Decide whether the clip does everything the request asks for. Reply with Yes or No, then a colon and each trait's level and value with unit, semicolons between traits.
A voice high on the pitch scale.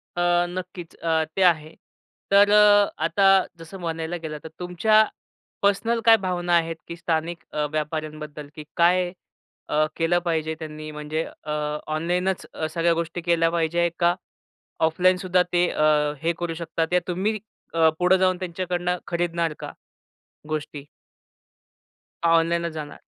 No: medium, 170 Hz